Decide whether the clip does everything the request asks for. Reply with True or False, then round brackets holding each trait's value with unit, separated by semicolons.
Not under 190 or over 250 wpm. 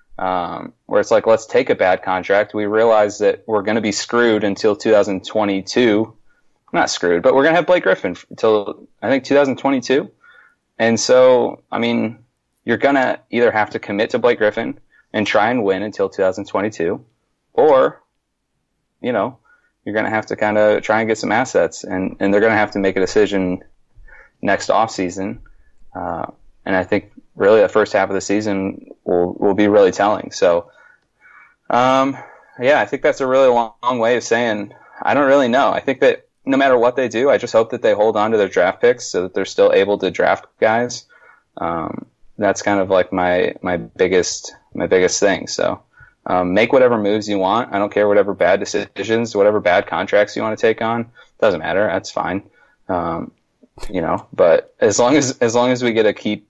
True (200 wpm)